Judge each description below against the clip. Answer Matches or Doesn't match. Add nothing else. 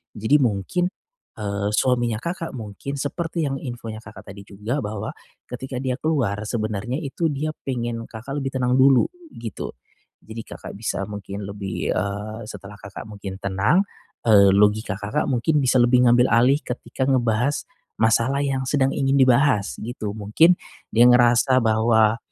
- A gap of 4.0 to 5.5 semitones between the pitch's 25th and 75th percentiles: Matches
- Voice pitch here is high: Doesn't match